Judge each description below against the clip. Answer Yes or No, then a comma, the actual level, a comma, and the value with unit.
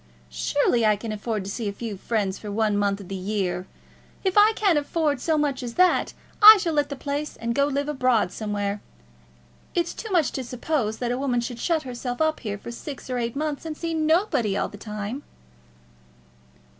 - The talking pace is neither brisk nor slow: No, fast, 215 wpm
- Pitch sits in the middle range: No, high, 245 Hz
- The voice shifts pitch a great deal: Yes, wide, 6.2 semitones